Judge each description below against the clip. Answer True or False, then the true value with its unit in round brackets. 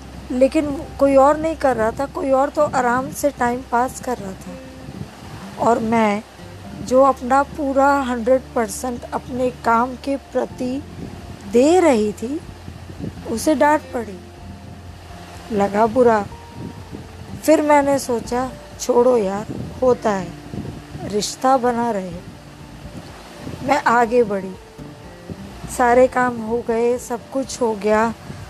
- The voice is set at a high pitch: True (245 Hz)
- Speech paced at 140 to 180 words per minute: False (120 wpm)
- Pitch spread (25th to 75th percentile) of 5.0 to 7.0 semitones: False (3.9 semitones)